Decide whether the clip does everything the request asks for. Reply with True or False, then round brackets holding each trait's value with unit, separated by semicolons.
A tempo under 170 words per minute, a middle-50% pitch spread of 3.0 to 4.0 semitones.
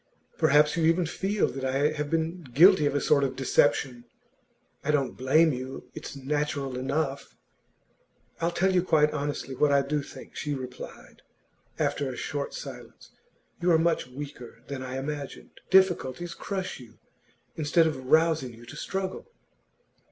True (155 wpm; 3.5 semitones)